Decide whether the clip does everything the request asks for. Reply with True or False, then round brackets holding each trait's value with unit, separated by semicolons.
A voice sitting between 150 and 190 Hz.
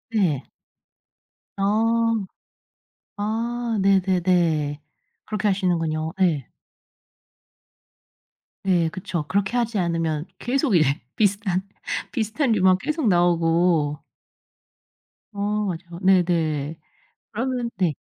True (185 Hz)